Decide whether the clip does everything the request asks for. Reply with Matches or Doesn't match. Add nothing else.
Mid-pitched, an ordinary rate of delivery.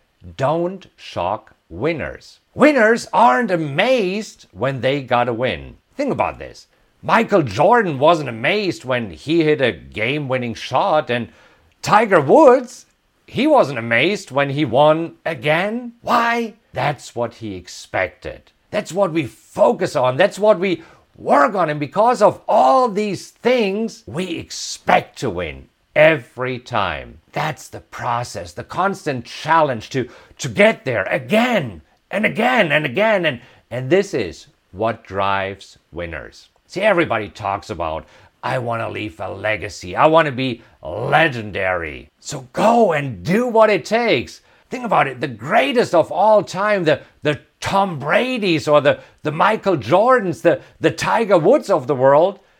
Matches